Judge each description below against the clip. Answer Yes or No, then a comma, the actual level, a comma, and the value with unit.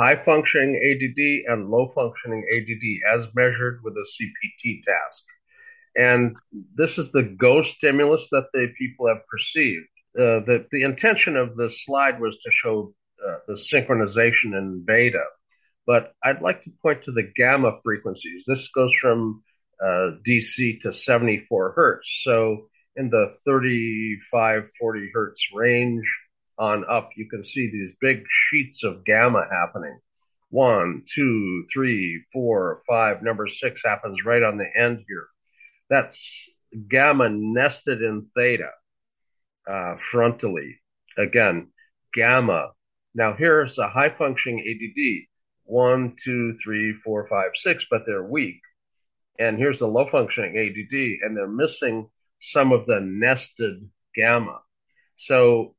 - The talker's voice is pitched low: Yes, low, 120 Hz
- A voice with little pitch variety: No, average, 3.4 semitones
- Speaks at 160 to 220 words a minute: No, slow, 135 wpm